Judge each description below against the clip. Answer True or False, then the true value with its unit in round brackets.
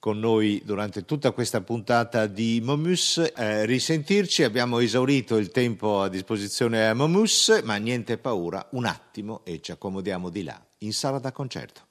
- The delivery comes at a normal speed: True (160 wpm)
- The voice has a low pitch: True (115 Hz)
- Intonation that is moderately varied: True (4.1 semitones)